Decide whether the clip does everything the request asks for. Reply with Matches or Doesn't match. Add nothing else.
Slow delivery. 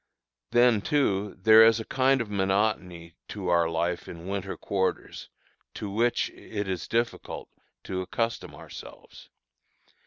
Matches